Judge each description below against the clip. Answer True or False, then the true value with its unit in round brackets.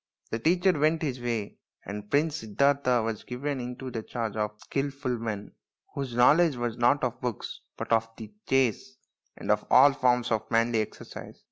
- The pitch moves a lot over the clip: False (3.7 semitones)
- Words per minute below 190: True (175 wpm)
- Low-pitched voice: True (125 Hz)